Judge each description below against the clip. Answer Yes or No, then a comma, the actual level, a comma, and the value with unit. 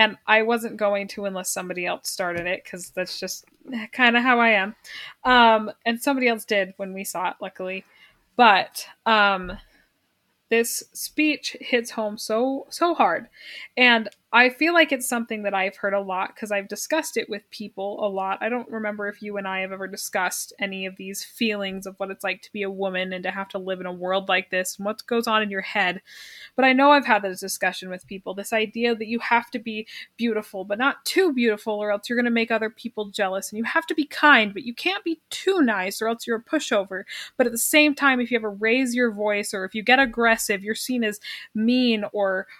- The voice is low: No, high, 215 Hz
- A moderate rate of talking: No, fast, 230 wpm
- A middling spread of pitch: Yes, average, 3.6 semitones